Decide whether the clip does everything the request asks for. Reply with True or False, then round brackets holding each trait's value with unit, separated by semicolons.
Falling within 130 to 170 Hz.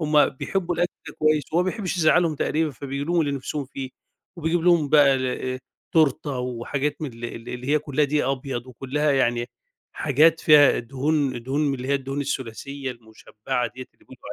True (140 Hz)